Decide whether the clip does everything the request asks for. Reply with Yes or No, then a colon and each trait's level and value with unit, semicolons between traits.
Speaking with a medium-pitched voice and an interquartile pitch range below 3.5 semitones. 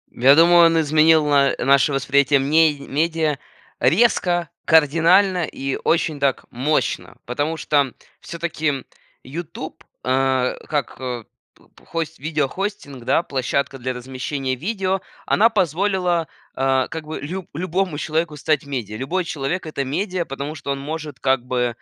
No: medium, 150 Hz; average, 3.8 semitones